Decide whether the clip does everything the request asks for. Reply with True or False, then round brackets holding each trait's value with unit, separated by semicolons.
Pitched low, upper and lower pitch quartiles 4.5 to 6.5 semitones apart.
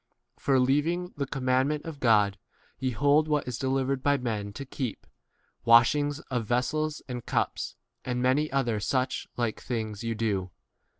False (130 Hz; 3.6 semitones)